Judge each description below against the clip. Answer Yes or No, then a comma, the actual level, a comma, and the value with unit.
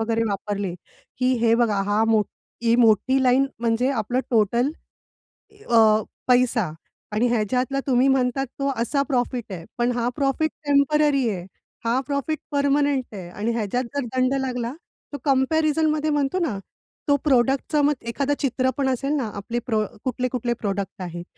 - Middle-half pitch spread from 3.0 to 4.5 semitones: Yes, average, 3.5 semitones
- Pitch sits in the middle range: No, very high, 250 Hz